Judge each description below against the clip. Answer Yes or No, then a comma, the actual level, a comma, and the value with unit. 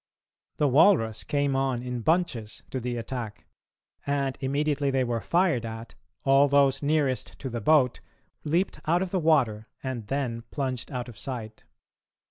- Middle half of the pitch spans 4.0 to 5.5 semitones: No, average, 3.4 semitones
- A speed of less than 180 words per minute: Yes, average, 155 wpm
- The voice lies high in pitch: No, low, 135 Hz